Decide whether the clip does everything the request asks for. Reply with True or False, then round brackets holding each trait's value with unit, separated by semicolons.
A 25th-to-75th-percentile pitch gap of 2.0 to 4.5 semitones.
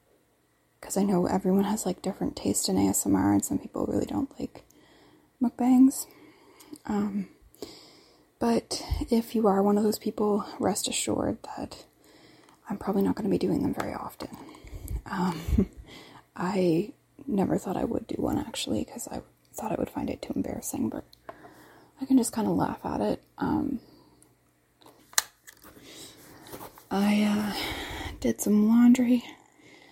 False (5.1 semitones)